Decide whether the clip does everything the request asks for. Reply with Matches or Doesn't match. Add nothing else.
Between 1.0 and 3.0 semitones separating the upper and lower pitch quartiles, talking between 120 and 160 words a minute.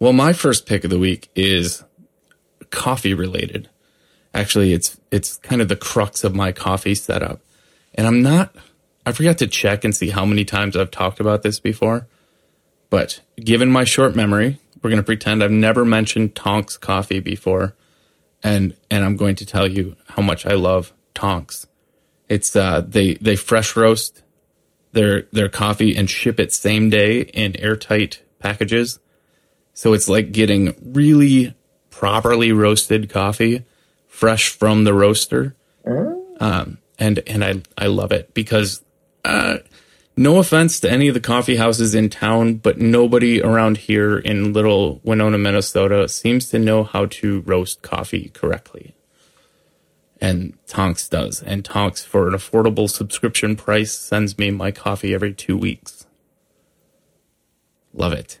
Matches